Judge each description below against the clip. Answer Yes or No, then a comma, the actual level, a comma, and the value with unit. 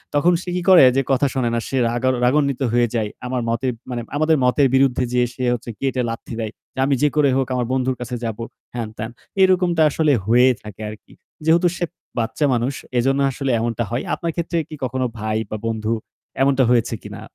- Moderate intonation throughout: Yes, average, 3.2 semitones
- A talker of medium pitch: No, low, 130 Hz